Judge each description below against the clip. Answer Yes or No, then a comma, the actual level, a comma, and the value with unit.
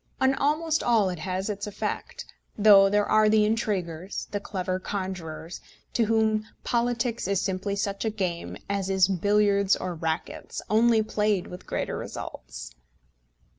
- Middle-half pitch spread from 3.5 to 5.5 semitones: No, average, 2.7 semitones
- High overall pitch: Yes, high, 200 Hz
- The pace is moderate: Yes, average, 145 wpm